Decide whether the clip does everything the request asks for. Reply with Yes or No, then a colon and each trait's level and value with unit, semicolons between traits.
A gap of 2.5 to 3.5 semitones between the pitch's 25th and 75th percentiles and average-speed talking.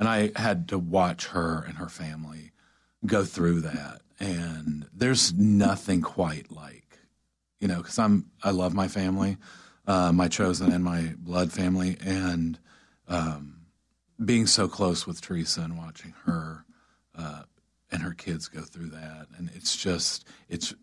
Yes: average, 3.0 semitones; average, 155 wpm